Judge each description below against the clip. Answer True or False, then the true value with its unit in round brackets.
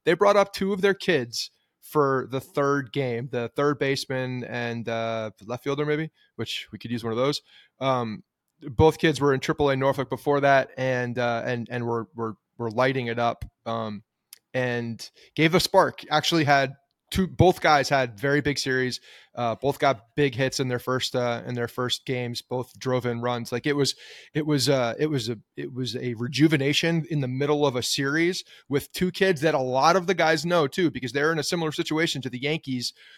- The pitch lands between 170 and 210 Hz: False (135 Hz)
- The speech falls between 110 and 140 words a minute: False (205 wpm)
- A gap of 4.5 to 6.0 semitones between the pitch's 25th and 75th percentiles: False (3.6 semitones)